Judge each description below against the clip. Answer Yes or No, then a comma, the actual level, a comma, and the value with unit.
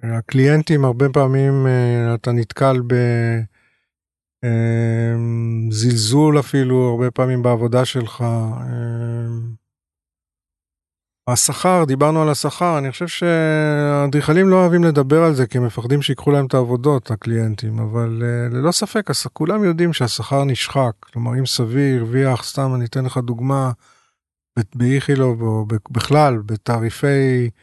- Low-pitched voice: Yes, low, 125 Hz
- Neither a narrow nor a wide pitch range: Yes, average, 3.5 semitones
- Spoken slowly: No, average, 115 wpm